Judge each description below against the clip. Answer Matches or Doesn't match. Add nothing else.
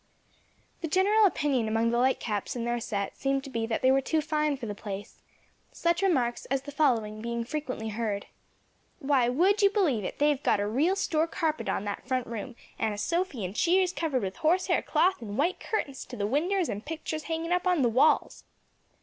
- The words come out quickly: Matches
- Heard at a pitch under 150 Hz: Doesn't match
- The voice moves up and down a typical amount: Doesn't match